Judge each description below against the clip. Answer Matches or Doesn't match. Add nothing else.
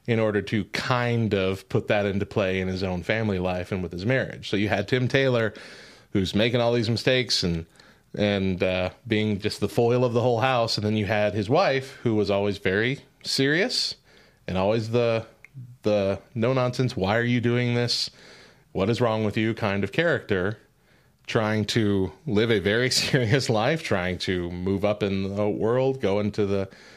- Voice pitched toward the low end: Matches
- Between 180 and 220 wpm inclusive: Matches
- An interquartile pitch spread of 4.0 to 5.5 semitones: Doesn't match